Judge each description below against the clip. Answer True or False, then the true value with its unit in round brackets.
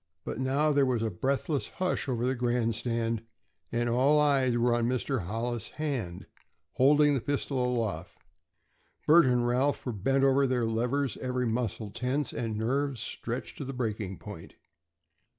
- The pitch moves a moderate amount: True (3.0 semitones)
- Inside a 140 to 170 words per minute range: True (155 wpm)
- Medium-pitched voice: False (125 Hz)